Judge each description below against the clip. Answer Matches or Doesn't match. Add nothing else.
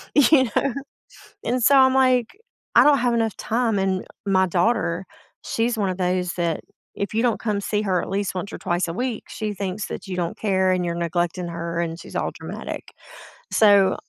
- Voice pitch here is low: Doesn't match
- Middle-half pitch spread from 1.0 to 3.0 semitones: Doesn't match